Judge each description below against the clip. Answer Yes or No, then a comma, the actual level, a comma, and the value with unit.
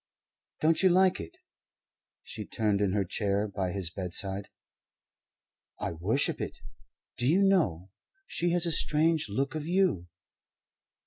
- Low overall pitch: Yes, low, 115 Hz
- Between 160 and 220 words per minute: No, slow, 135 wpm